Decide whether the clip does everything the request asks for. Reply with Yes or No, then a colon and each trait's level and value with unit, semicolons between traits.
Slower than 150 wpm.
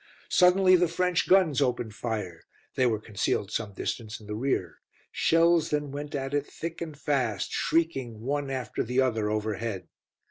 No: average, 165 wpm